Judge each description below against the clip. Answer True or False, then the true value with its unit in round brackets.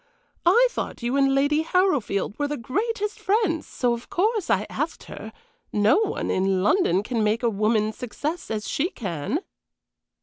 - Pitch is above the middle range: True (270 Hz)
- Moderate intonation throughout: False (9.0 semitones)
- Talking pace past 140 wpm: True (165 wpm)